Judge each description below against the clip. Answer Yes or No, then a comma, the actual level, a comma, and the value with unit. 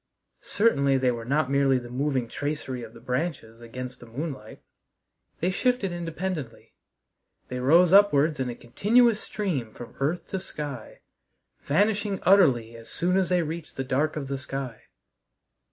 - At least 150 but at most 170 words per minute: Yes, average, 155 wpm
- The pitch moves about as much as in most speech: No, wide, 5.9 semitones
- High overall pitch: No, medium, 140 Hz